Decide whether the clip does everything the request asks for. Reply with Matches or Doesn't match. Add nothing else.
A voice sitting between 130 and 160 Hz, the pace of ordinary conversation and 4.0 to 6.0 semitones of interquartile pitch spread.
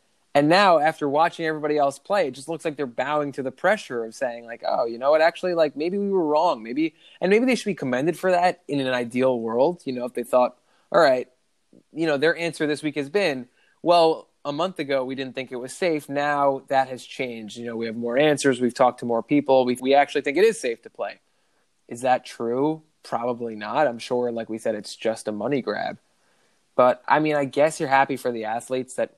Doesn't match